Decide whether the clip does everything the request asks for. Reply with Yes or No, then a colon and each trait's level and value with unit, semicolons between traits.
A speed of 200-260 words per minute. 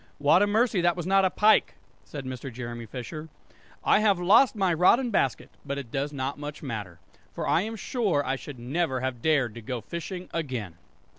Yes: fast, 205 wpm